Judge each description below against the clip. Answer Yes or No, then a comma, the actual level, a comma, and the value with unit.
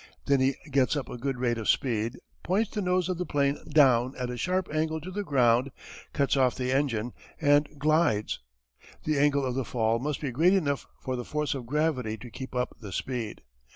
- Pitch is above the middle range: No, low, 135 Hz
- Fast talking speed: Yes, fast, 210 wpm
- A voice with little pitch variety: No, average, 3.7 semitones